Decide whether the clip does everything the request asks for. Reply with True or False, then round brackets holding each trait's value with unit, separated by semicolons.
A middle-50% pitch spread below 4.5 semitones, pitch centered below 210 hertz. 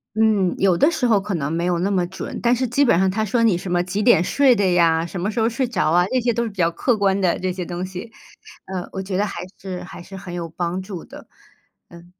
True (3.7 semitones; 190 Hz)